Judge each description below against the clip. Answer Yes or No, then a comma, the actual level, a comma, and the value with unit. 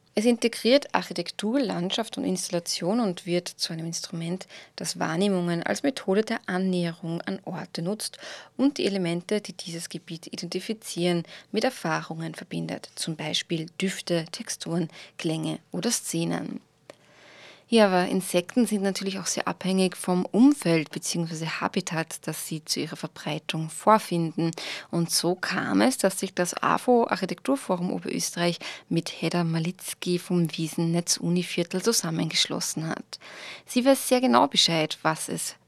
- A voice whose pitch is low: No, medium, 180 Hz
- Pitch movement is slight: No, average, 3.4 semitones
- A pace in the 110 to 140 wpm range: Yes, average, 135 wpm